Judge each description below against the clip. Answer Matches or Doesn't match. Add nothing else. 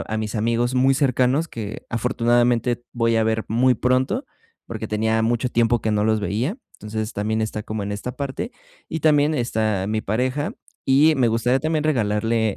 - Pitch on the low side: Matches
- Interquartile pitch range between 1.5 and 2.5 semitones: Doesn't match